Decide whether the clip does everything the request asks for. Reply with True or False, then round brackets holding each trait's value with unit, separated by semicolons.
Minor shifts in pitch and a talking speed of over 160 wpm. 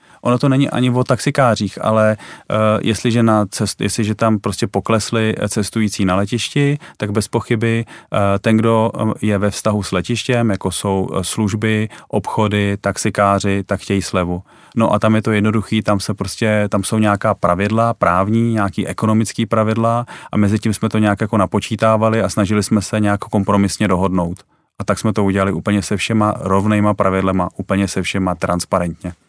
True (2.0 semitones; 170 wpm)